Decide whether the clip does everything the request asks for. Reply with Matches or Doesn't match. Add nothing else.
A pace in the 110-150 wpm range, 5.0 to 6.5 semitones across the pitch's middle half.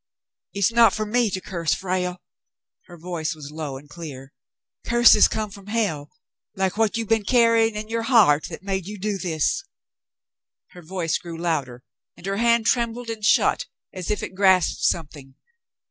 Doesn't match